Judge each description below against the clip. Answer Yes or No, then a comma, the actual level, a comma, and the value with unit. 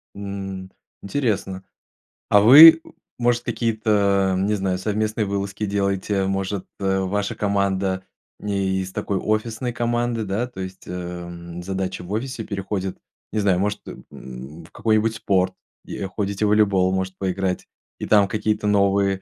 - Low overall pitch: Yes, low, 100 Hz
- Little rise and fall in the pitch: Yes, narrow, 2.1 semitones